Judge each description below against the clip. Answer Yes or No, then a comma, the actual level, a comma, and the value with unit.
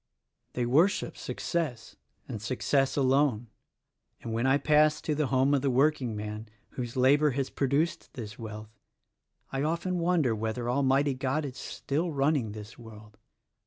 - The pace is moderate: Yes, average, 145 wpm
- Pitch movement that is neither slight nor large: Yes, average, 4.3 semitones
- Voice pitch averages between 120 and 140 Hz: Yes, low, 135 Hz